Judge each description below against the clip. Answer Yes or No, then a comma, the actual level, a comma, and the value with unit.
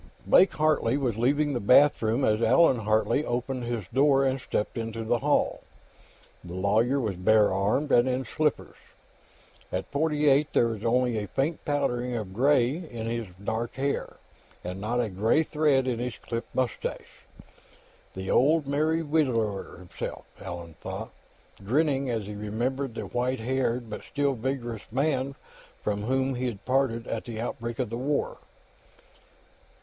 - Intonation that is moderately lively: Yes, average, 3.7 semitones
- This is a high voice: No, low, 125 Hz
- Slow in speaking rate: No, average, 155 wpm